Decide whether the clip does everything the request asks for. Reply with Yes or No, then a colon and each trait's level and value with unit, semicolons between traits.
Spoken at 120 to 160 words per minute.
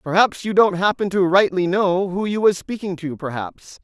No: fast, 205 wpm